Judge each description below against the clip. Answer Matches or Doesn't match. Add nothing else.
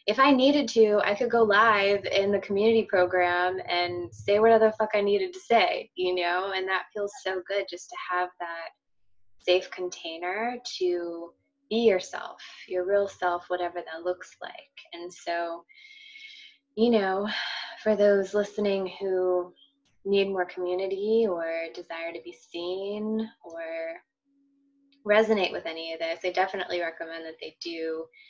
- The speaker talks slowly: Doesn't match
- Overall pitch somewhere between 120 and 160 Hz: Doesn't match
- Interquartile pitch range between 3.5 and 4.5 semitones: Matches